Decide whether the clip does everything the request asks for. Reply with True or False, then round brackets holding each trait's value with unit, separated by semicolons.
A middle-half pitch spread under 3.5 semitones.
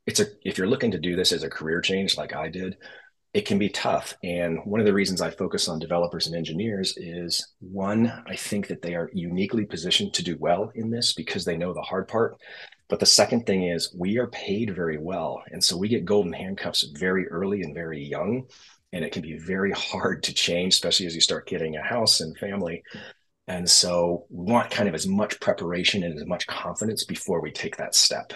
True (2.7 semitones)